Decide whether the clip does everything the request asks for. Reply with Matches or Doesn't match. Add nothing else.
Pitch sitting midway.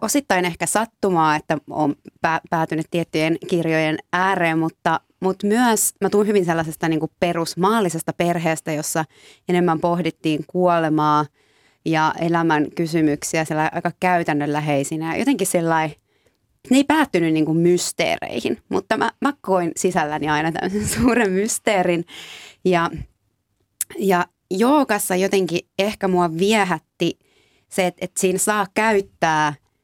Matches